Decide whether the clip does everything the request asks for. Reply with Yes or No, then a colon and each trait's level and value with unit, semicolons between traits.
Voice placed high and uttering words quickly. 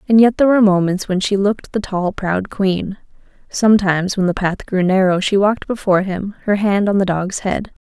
Yes: high, 195 Hz; fast, 215 wpm